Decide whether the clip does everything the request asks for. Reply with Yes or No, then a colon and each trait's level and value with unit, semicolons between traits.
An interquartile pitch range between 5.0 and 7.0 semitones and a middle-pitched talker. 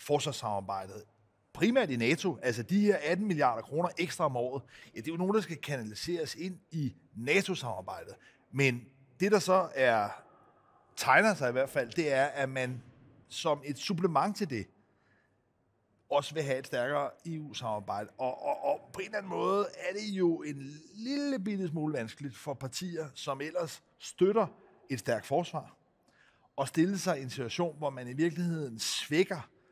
Yes: wide, 5.6 semitones; medium, 145 Hz